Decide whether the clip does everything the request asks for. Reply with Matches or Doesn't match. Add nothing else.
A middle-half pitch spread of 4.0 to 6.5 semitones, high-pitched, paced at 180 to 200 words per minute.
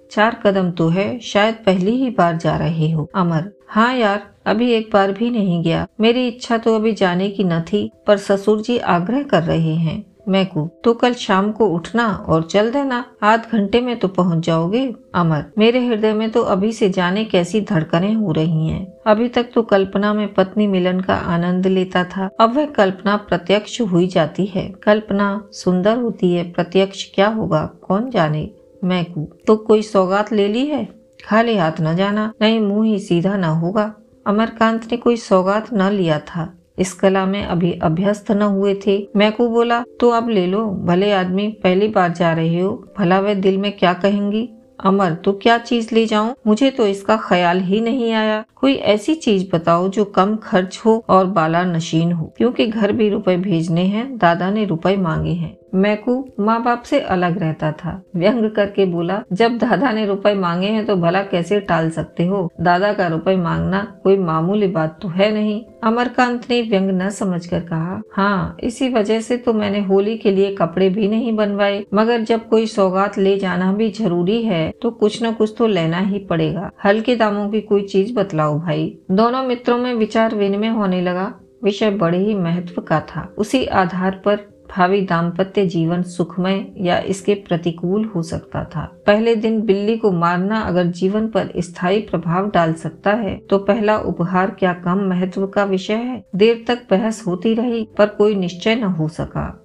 Doesn't match